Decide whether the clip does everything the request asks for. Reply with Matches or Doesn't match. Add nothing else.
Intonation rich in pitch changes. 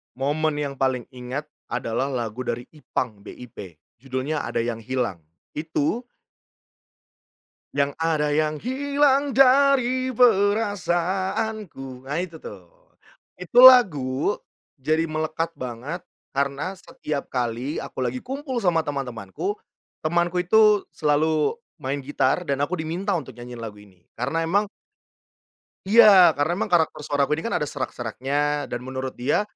Matches